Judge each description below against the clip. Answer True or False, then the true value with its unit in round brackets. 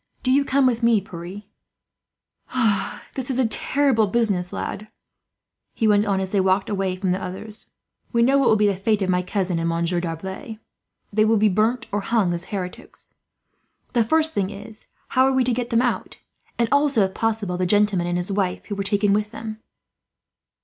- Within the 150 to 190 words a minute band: False (200 wpm)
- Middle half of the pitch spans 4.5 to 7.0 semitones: False (3.5 semitones)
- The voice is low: False (210 Hz)